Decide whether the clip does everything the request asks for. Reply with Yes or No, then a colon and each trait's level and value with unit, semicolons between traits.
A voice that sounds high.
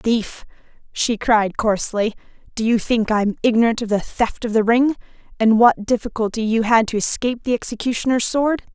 Yes: high, 230 Hz